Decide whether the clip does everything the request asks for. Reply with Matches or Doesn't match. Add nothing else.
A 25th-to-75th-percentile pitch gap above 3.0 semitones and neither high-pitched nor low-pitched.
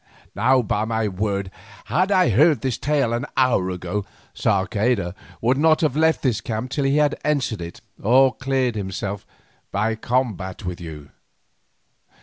Doesn't match